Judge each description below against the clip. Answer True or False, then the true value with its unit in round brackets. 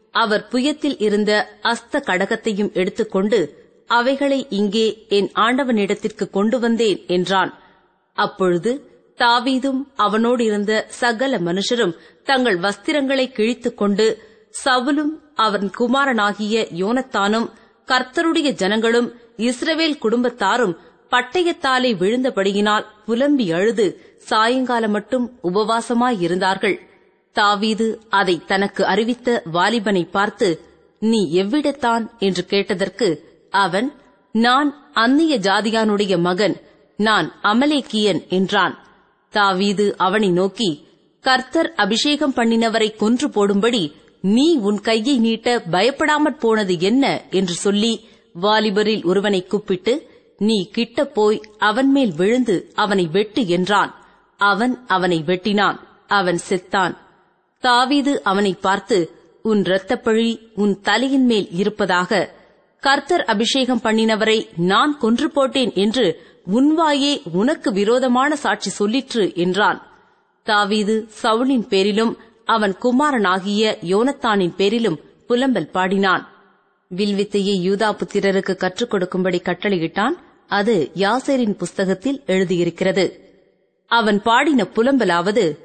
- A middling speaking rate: True (95 wpm)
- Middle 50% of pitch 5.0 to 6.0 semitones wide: False (4.1 semitones)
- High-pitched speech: True (220 Hz)